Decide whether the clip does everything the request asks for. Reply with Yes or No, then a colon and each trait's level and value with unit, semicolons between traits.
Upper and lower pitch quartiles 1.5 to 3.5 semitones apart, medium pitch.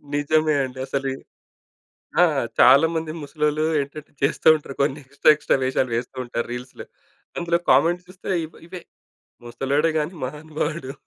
Yes: average, 2.9 semitones; medium, 150 Hz